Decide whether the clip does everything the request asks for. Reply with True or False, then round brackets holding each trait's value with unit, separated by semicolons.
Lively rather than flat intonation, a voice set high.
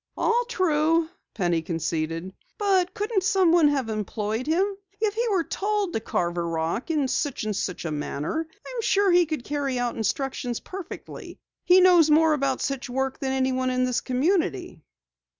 True (8.4 semitones; 280 Hz)